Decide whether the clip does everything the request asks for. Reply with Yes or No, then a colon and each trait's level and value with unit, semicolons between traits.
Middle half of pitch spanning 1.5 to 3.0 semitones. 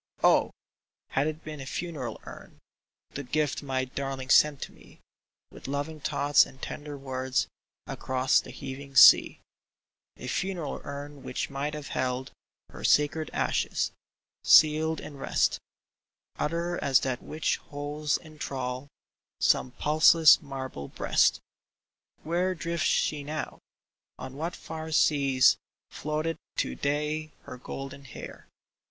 Yes: average, 2.7 semitones